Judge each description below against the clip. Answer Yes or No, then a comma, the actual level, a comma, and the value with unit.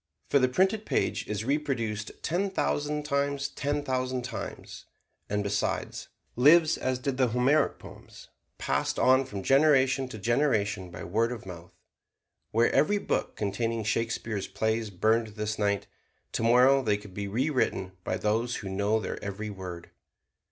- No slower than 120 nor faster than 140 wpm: No, average, 150 wpm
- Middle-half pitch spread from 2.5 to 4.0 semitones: No, average, 4.9 semitones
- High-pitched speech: No, low, 115 Hz